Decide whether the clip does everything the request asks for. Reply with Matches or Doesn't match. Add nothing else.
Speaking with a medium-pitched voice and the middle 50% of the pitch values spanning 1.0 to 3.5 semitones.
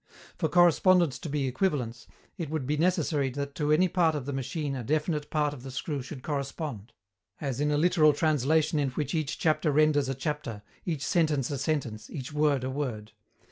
Matches